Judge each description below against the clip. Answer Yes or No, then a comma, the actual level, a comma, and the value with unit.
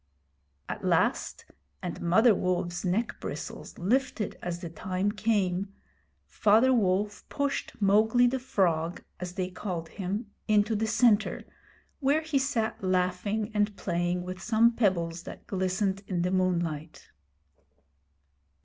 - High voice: Yes, high, 195 Hz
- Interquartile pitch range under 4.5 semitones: Yes, average, 3.5 semitones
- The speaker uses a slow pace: Yes, slow, 125 wpm